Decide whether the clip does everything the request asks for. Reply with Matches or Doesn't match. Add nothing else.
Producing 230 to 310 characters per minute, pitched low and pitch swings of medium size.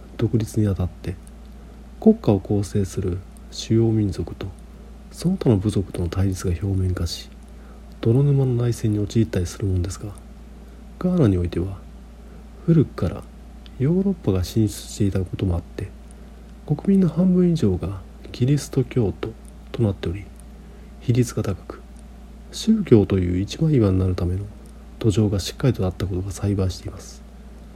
Matches